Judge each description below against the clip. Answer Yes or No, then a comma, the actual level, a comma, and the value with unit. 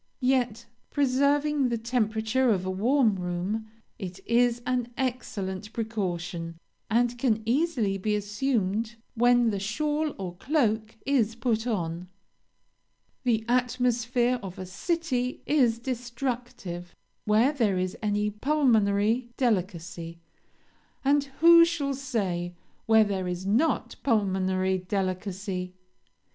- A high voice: Yes, high, 225 Hz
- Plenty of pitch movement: No, average, 4.7 semitones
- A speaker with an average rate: No, slow, 110 wpm